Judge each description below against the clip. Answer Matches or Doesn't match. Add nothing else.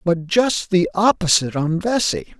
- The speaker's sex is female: Doesn't match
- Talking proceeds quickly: Doesn't match